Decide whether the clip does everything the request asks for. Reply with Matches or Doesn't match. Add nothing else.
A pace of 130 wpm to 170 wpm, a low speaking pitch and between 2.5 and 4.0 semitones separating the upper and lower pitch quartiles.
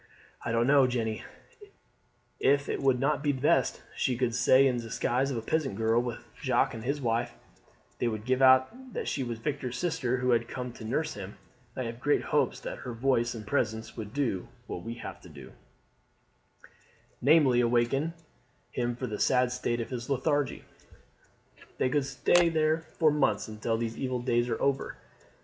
Doesn't match